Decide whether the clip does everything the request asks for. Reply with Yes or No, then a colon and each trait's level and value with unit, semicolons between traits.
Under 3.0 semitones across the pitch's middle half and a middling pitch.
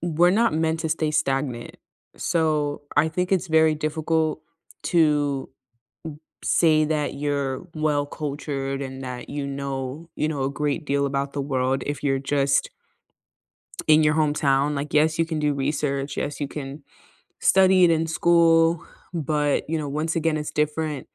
Yes: narrow, 2.4 semitones; medium, 150 Hz